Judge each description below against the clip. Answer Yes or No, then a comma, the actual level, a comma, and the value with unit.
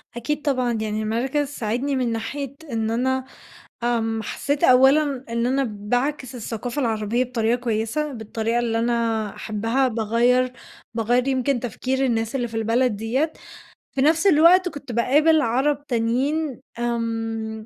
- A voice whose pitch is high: Yes, high, 240 Hz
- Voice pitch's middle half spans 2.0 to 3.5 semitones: Yes, average, 3.2 semitones